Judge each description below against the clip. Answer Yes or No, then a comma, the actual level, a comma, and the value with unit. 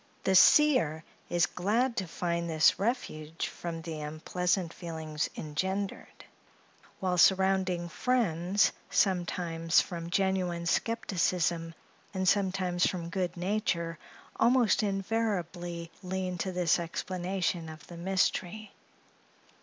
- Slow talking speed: Yes, slow, 105 wpm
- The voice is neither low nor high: Yes, medium, 180 Hz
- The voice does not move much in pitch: Yes, narrow, 2.3 semitones